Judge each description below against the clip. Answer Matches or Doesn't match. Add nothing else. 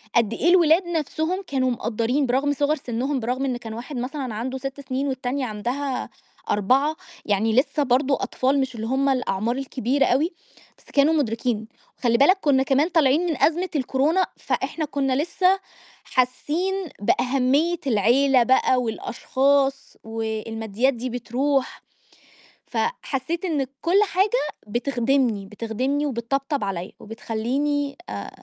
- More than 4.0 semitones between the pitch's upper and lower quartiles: Doesn't match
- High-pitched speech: Matches